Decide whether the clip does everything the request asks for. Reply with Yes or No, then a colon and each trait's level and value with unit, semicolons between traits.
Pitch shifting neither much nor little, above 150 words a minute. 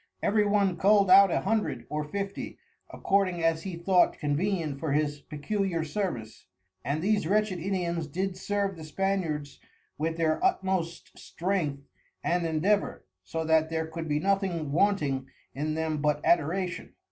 No: average, 4.1 semitones; average, 145 wpm